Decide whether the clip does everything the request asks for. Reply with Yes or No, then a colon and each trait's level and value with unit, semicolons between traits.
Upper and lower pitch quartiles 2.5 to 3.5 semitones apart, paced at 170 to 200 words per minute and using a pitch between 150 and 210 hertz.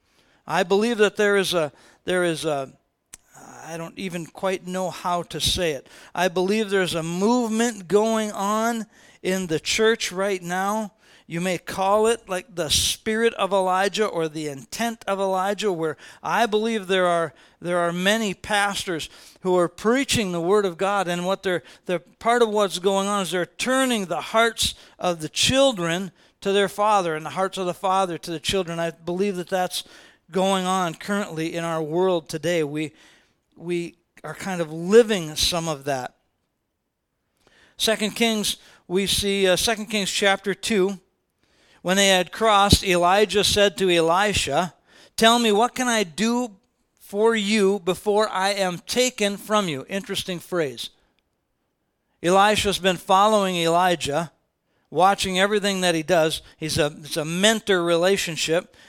No: average, 3.2 semitones; average, 160 wpm; high, 190 Hz